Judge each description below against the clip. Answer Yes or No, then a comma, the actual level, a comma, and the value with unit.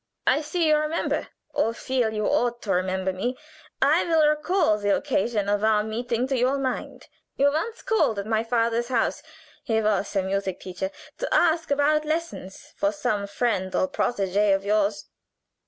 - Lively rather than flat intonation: Yes, wide, 6.0 semitones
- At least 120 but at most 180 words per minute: Yes, average, 170 wpm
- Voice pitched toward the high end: Yes, high, 230 Hz